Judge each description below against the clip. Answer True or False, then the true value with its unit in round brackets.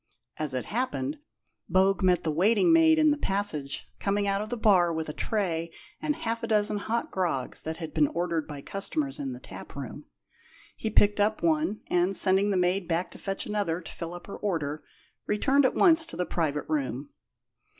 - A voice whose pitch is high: True (195 Hz)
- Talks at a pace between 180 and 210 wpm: True (200 wpm)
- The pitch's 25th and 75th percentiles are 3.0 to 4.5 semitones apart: False (5.4 semitones)